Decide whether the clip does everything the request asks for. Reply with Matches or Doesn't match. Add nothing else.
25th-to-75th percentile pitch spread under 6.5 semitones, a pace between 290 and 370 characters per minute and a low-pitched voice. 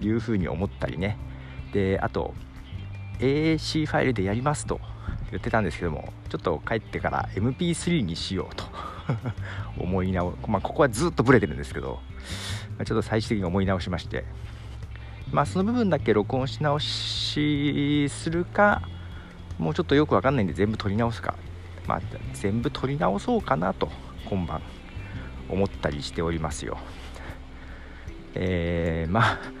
Matches